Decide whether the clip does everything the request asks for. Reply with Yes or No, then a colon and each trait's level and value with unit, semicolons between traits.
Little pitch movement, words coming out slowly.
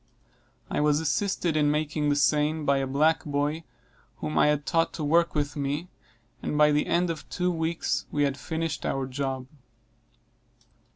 No: narrow, 1.9 semitones; average, 170 wpm